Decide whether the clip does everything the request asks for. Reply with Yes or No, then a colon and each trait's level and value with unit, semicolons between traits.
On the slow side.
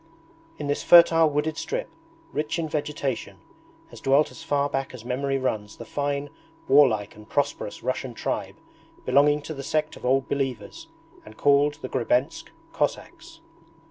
No: average, 150 wpm